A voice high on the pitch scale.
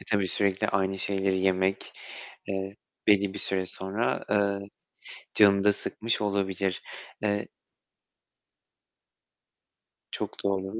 No: low, 100 Hz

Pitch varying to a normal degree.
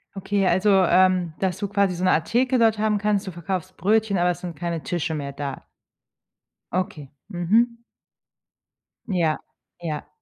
Yes: average, 3.3 semitones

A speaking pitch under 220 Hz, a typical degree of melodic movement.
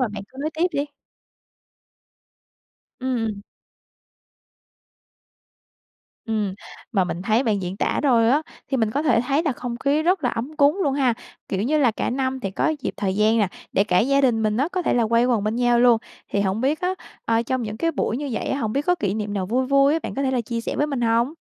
No: high, 245 Hz; average, 4.4 semitones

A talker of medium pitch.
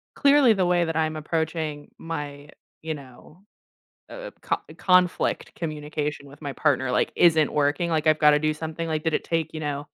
Yes: medium, 155 Hz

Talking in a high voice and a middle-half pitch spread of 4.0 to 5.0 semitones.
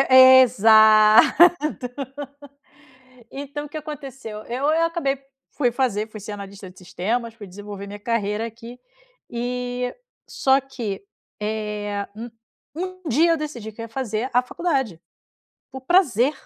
Yes: high, 235 Hz; average, 4.3 semitones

